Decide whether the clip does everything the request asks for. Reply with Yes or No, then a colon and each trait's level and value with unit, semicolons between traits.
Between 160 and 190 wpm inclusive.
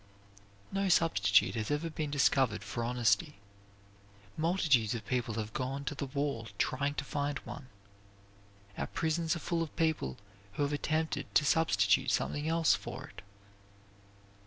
No: average, 150 wpm